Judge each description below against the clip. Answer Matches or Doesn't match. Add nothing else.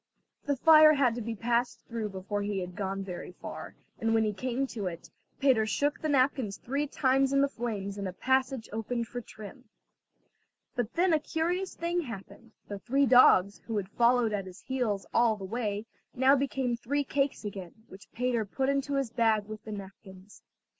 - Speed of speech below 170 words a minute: Doesn't match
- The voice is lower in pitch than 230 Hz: Doesn't match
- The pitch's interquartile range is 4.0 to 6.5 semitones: Matches